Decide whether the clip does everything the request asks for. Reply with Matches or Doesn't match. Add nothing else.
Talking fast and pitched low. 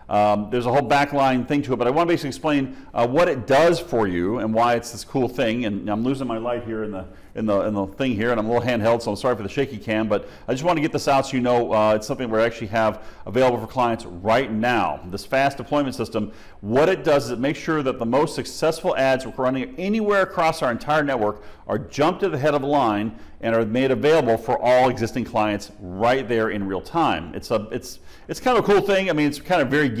Matches